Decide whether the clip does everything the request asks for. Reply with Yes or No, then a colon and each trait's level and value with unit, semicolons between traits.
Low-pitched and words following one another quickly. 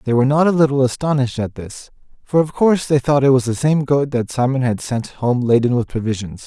Yes: low, 130 Hz; fast, 240 wpm